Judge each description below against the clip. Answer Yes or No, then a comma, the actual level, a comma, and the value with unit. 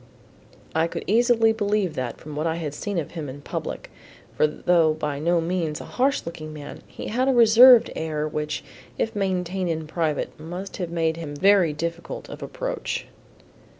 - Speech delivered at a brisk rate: No, average, 180 wpm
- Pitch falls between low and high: Yes, medium, 170 Hz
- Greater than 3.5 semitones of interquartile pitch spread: Yes, average, 4.8 semitones